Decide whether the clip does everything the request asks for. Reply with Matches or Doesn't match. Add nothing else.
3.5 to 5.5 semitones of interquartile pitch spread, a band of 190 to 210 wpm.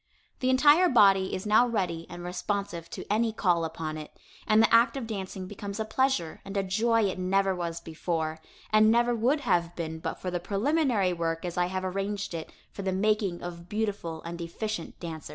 Matches